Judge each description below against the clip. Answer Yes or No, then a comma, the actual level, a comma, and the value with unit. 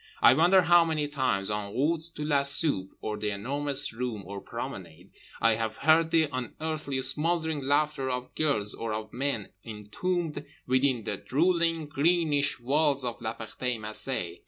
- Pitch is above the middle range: No, low, 135 Hz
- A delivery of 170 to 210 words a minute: No, average, 155 wpm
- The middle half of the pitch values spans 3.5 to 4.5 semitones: No, wide, 5.6 semitones